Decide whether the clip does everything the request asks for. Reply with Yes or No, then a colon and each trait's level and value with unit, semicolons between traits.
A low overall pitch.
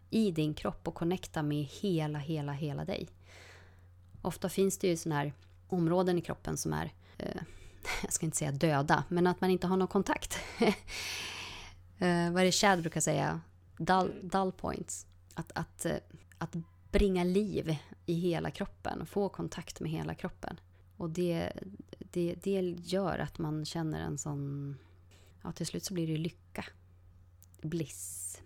No: medium, 155 Hz